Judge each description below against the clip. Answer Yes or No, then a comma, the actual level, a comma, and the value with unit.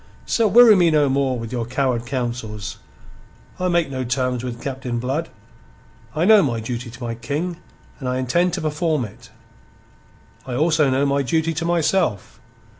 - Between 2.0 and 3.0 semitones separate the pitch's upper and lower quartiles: No, average, 5.0 semitones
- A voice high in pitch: No, low, 135 Hz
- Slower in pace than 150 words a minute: No, average, 170 wpm